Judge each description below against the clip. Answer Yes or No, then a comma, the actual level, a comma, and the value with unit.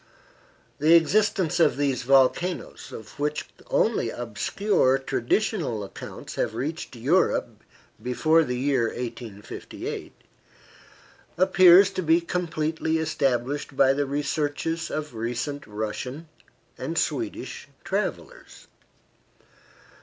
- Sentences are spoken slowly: Yes, slow, 95 wpm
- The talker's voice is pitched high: No, medium, 145 Hz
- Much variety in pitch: No, average, 4.7 semitones